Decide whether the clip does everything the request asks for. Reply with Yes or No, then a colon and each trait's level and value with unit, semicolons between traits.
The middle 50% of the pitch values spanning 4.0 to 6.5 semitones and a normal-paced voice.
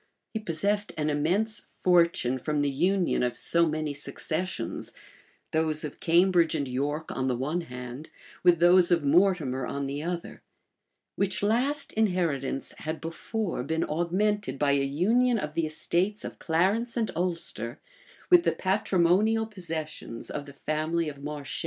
Yes: average, 4.4 semitones; average, 150 wpm